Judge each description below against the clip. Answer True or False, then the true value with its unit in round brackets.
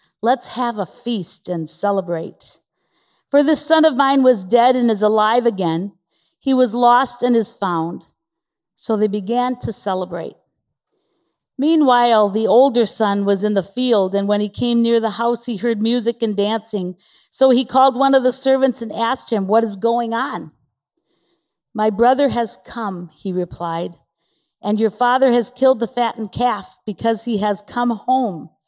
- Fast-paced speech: False (170 wpm)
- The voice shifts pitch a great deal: False (3.5 semitones)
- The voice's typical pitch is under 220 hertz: False (230 Hz)